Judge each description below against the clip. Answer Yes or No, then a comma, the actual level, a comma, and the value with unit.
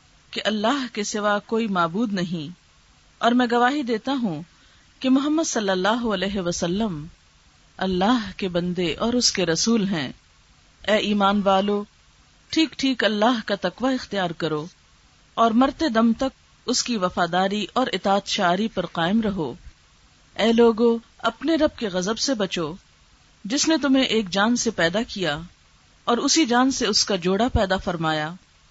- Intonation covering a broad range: No, average, 4.6 semitones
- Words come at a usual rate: Yes, average, 155 wpm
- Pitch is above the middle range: Yes, high, 210 Hz